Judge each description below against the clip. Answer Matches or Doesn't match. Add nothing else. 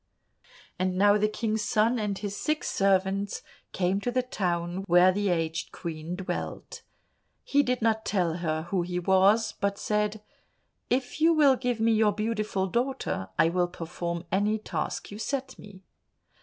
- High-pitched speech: Matches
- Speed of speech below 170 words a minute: Matches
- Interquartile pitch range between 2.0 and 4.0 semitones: Matches